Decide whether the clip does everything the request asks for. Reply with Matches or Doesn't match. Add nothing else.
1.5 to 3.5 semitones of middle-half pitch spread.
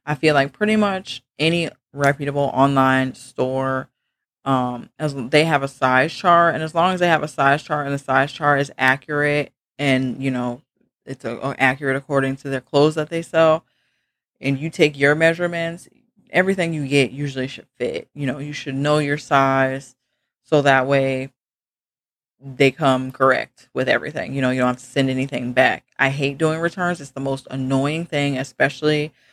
Matches